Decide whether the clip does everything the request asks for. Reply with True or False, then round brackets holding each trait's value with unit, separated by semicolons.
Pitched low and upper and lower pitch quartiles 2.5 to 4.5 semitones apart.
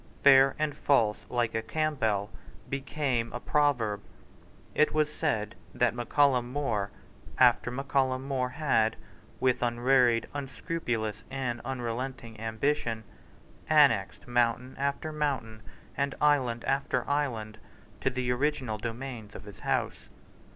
True (125 Hz; 3.6 semitones)